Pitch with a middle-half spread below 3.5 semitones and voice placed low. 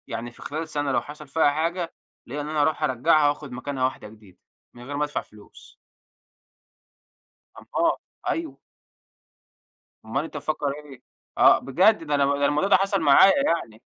No: average, 2.9 semitones; medium, 145 Hz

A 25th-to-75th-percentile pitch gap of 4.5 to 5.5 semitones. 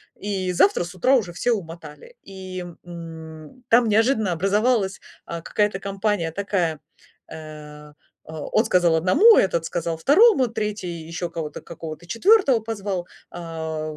Yes: average, 4.8 semitones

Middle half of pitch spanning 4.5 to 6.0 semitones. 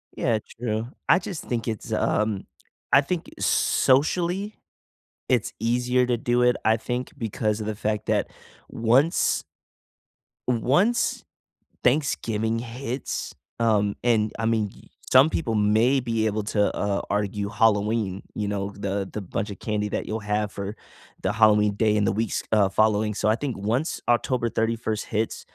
No: average, 2.8 semitones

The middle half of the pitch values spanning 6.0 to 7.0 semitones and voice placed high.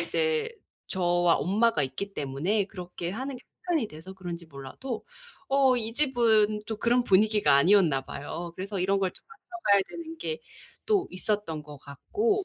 Yes: wide, 6.3 semitones; high, 205 Hz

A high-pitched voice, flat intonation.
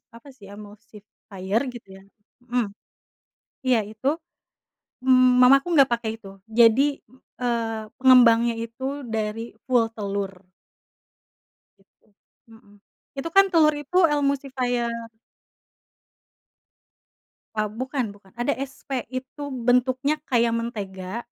No: high, 235 Hz; average, 3.4 semitones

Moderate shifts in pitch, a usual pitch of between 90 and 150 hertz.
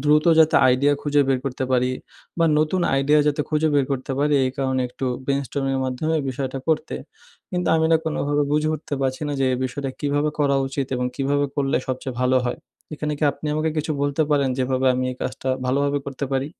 No: narrow, 2.3 semitones; medium, 140 Hz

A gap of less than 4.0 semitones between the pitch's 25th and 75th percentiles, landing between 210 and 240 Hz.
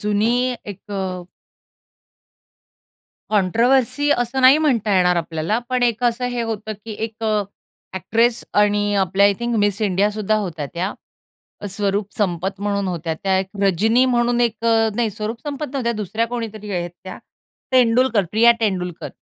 Yes: average, 3.3 semitones; high, 215 Hz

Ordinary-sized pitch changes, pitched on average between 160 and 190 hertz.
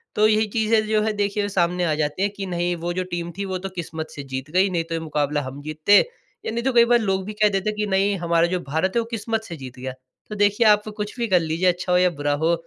Yes: average, 4.5 semitones; medium, 185 Hz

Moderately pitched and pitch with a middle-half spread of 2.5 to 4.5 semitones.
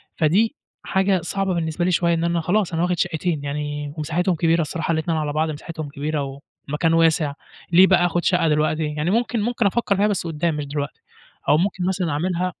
Yes: medium, 165 Hz; average, 3.0 semitones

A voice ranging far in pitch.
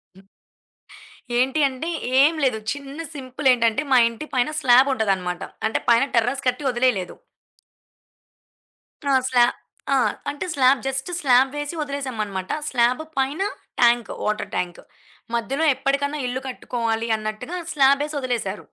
No: average, 3.2 semitones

